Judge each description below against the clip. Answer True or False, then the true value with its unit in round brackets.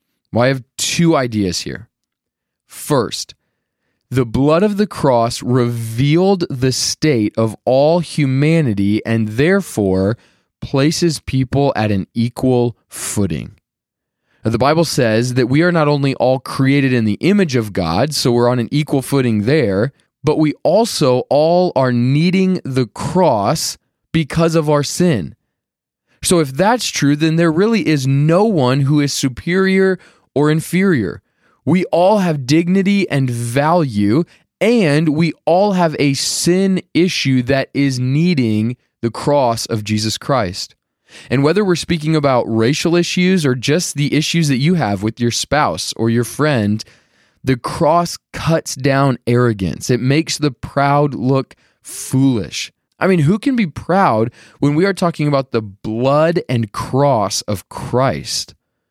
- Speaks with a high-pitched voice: False (140 Hz)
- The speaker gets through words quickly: False (150 wpm)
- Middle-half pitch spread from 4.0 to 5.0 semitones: False (5.4 semitones)